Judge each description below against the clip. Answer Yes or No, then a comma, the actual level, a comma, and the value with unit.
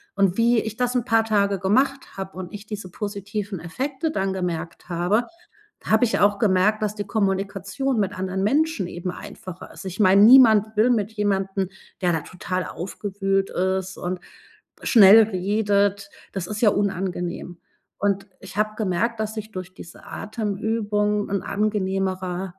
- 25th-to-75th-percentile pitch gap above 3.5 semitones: No, narrow, 2.4 semitones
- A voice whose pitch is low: No, high, 200 Hz